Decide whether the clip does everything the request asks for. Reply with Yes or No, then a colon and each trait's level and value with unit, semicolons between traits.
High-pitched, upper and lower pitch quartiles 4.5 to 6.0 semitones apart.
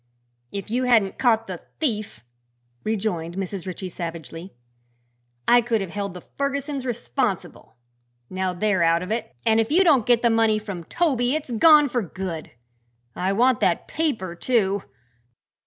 Yes: high, 215 Hz; average, 4.8 semitones